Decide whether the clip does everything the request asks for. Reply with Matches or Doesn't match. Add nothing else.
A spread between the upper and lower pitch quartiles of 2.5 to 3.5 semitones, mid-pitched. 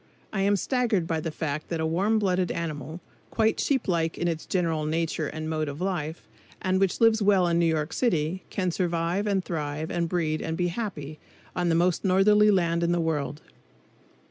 Matches